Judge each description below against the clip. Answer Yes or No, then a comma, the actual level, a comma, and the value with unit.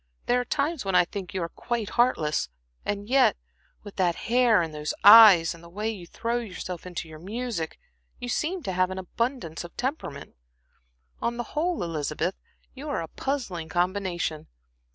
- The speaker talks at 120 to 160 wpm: No, average, 175 wpm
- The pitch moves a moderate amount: No, wide, 6.1 semitones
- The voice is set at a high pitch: Yes, high, 195 Hz